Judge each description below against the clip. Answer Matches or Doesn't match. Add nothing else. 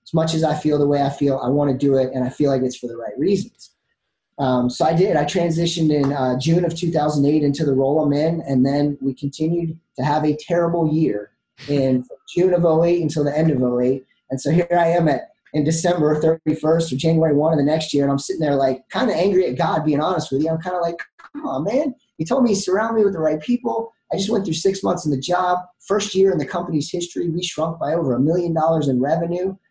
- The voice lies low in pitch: Doesn't match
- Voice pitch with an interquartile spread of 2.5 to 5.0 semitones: Matches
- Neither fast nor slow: Doesn't match